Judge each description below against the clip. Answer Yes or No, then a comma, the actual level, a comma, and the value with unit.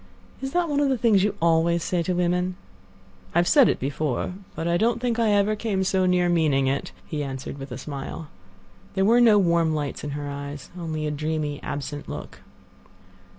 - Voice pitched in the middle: Yes, medium, 170 Hz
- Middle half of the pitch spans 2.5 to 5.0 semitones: No, wide, 5.6 semitones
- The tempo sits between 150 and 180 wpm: No, average, 200 wpm